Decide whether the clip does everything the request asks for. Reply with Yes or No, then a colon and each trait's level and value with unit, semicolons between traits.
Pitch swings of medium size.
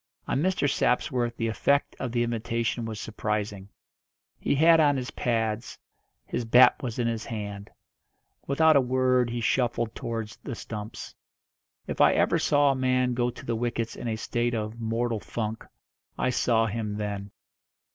No: narrow, 2.3 semitones